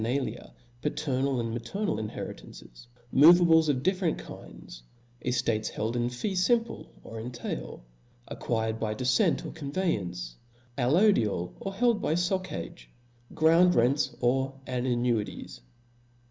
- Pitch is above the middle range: No, low, 130 Hz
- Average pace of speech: No, slow, 130 wpm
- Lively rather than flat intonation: Yes, wide, 6.8 semitones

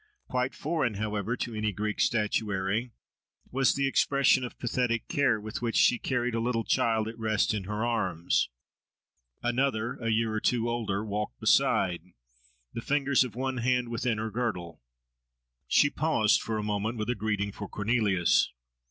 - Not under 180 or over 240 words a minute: No, average, 160 wpm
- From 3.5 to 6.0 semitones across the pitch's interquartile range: No, average, 2.7 semitones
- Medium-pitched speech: No, low, 115 Hz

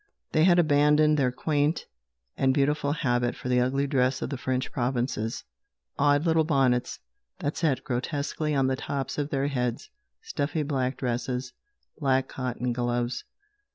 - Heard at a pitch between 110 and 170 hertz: Yes, low, 135 Hz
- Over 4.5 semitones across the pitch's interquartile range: No, average, 2.7 semitones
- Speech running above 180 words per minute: No, average, 150 wpm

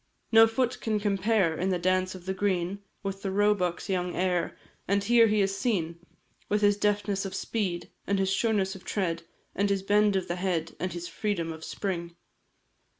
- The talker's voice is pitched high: Yes, high, 195 Hz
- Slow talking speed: No, average, 190 wpm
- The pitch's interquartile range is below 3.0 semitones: Yes, narrow, 2.4 semitones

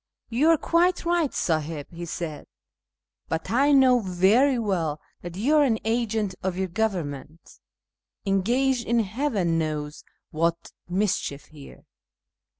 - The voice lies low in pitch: No, high, 195 Hz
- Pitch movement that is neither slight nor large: No, wide, 7.0 semitones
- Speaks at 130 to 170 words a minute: Yes, average, 145 wpm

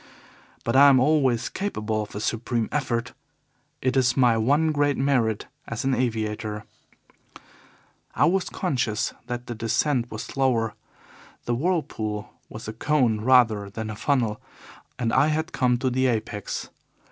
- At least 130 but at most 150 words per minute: Yes, average, 145 wpm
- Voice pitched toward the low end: Yes, low, 120 Hz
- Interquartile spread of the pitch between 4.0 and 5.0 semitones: No, average, 3.5 semitones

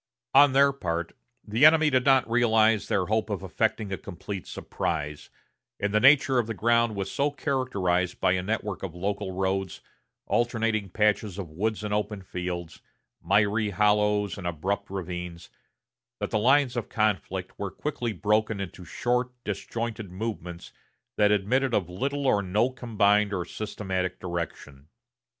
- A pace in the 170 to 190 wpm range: No, average, 150 wpm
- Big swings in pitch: No, average, 3.9 semitones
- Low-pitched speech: Yes, low, 105 Hz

